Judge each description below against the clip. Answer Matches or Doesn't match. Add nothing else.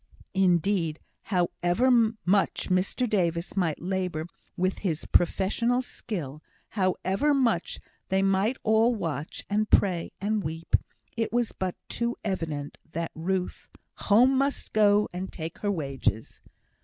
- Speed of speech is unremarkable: Doesn't match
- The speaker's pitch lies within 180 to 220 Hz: Matches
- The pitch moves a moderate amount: Matches